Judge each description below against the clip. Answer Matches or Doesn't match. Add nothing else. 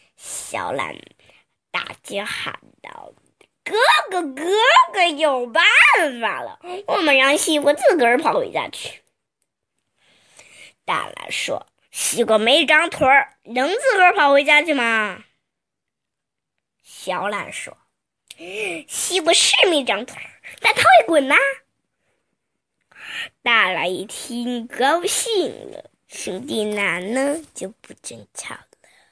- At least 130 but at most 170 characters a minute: Matches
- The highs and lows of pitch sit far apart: Matches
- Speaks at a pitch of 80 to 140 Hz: Doesn't match